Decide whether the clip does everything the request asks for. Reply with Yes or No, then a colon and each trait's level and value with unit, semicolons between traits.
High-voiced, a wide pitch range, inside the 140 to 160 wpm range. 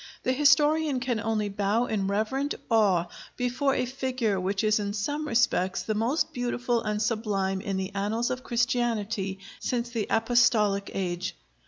No: high, 225 Hz; average, 3.6 semitones; average, 155 wpm